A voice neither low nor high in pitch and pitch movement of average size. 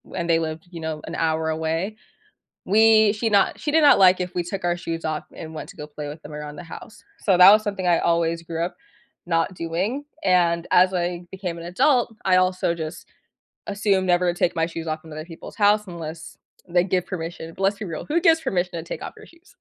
Yes: medium, 175 Hz; average, 3.1 semitones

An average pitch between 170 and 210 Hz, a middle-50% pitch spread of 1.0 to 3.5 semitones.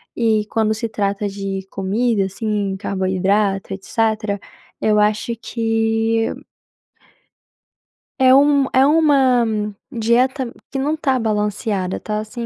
No: high, 220 Hz; average, 3.1 semitones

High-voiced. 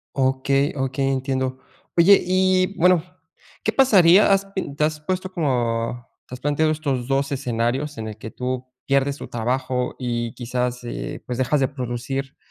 No: low, 135 Hz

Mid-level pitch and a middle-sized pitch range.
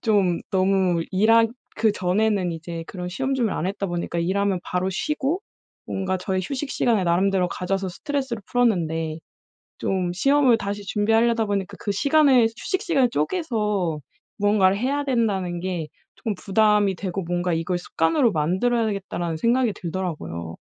No: high, 195 Hz; average, 4.4 semitones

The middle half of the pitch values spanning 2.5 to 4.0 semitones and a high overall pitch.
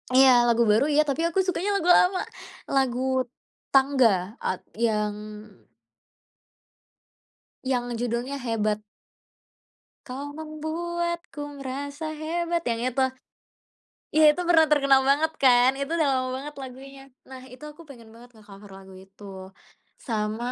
No: average, 4.6 semitones; very high, 270 Hz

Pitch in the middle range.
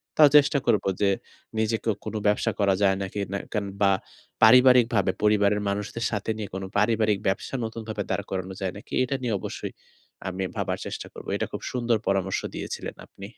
No: low, 105 Hz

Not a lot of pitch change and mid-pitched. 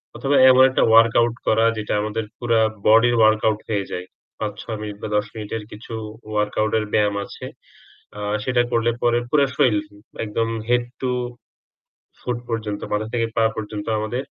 No: narrow, 2.0 semitones; low, 110 Hz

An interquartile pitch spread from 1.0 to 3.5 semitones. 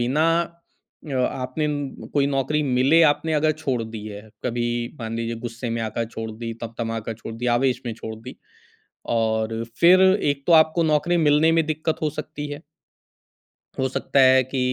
No: average, 5.0 semitones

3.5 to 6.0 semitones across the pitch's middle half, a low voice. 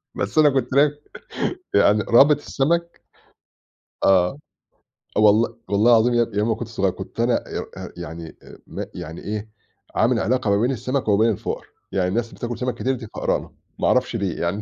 Yes: average, 3.9 semitones; low, 115 Hz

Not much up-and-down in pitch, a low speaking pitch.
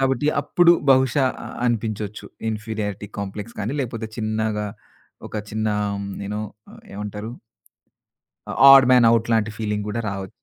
Yes: narrow, 2.1 semitones; low, 110 Hz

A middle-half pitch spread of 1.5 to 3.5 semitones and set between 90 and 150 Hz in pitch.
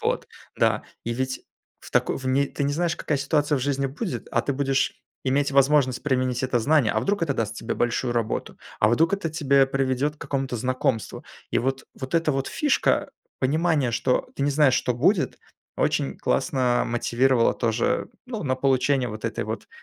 Yes: narrow, 2.6 semitones; low, 135 Hz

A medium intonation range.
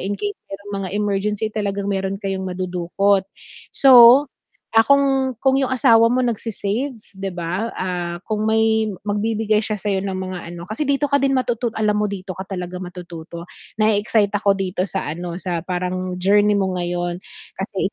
Yes: average, 3.1 semitones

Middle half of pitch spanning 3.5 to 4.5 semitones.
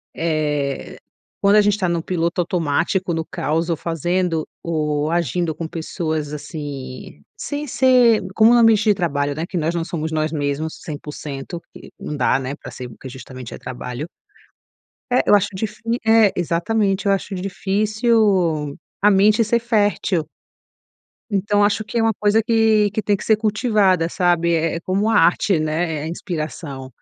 No: average, 5.1 semitones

